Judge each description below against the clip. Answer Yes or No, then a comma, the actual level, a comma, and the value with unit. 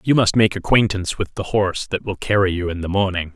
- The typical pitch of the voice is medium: No, very low, 95 Hz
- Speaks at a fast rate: Yes, fast, 250 wpm